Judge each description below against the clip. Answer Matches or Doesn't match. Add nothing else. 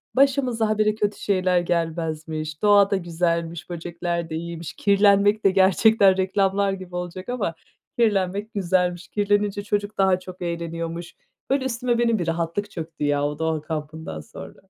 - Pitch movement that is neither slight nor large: Matches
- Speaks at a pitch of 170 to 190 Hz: Matches